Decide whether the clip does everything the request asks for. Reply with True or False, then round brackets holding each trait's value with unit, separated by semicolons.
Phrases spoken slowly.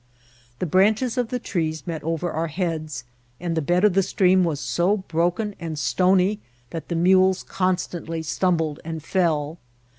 False (160 wpm)